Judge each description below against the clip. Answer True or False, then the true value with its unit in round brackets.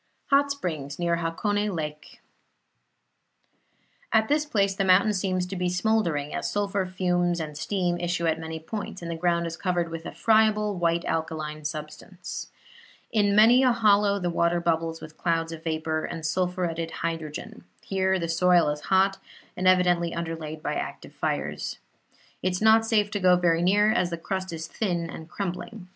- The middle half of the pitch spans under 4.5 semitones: True (3.3 semitones)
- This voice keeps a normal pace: True (170 wpm)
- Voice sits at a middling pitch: True (175 Hz)